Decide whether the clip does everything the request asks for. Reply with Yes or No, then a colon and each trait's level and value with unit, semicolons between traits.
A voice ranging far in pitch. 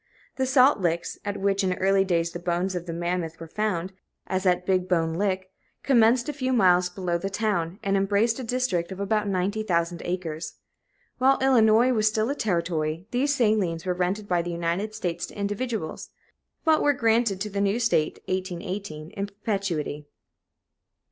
No: average, 3.9 semitones